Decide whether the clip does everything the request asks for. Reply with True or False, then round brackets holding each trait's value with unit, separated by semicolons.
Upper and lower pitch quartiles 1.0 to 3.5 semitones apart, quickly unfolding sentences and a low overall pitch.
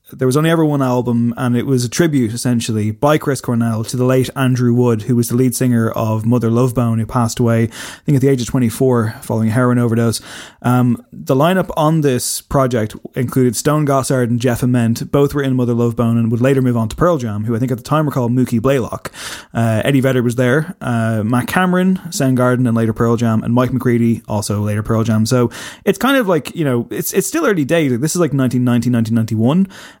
True (2.8 semitones; 235 wpm; 125 Hz)